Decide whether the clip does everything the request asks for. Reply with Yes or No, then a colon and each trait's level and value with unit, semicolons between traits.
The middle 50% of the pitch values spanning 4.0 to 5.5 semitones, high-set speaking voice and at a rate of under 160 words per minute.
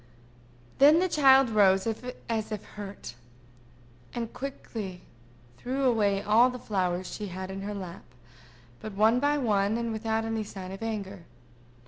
No: average, 3.6 semitones; high, 215 Hz; average, 145 wpm